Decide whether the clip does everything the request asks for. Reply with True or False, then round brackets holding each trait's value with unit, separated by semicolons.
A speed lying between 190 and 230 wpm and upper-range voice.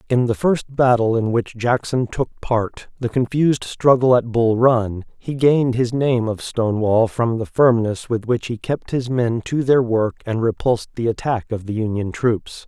False (195 wpm; 120 Hz)